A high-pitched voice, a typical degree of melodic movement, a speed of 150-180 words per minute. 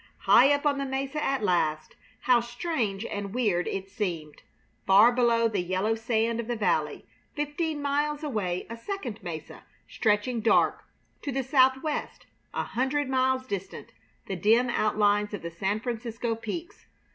Yes: high, 230 Hz; average, 4.7 semitones; average, 155 wpm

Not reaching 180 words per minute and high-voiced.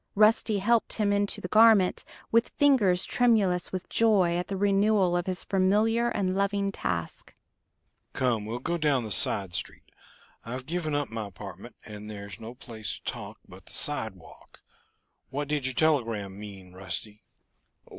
No: average, 155 wpm; medium, 175 Hz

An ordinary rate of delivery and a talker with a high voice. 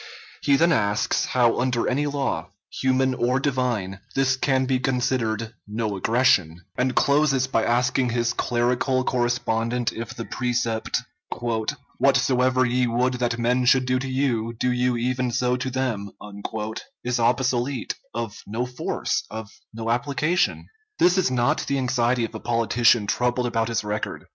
No: average, 150 wpm; low, 125 Hz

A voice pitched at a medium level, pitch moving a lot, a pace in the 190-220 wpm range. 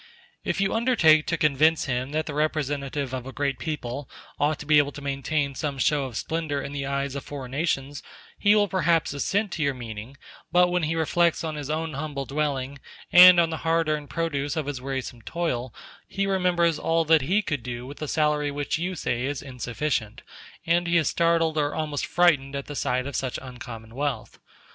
No: medium, 145 Hz; average, 3.2 semitones; fast, 205 wpm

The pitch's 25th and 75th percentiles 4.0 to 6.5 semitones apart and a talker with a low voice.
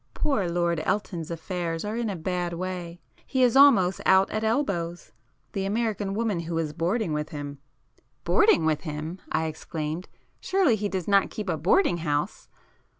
No: average, 4.4 semitones; medium, 180 Hz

